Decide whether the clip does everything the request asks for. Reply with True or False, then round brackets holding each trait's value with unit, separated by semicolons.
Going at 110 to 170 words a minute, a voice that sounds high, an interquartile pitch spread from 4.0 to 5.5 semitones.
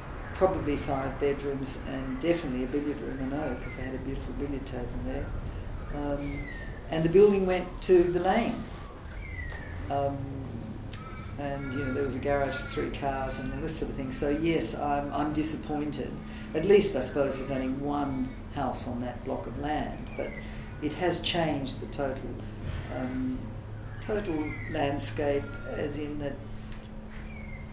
False (160 wpm; 135 Hz; 4.7 semitones)